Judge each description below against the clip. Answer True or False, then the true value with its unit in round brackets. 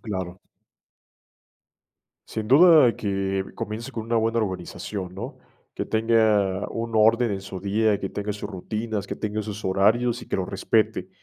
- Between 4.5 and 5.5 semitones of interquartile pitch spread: False (2.7 semitones)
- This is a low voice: True (105 Hz)